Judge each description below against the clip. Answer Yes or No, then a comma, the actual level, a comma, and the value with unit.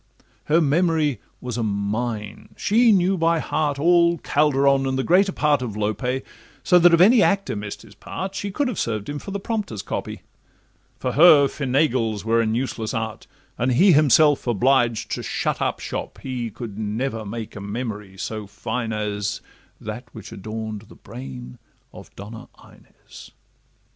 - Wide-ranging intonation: Yes, wide, 6.4 semitones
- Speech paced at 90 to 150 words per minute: No, average, 160 wpm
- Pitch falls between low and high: No, low, 125 Hz